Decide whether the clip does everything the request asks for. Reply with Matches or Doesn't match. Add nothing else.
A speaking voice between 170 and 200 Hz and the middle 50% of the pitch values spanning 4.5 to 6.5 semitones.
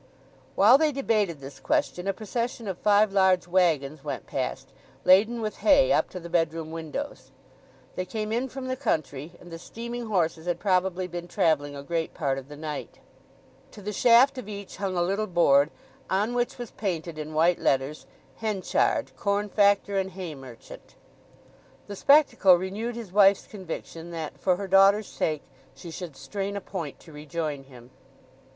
Matches